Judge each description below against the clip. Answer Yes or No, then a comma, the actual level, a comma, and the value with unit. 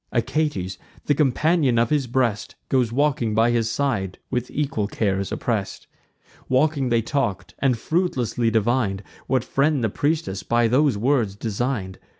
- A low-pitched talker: Yes, low, 120 Hz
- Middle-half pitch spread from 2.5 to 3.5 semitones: No, average, 4.1 semitones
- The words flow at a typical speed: Yes, average, 145 wpm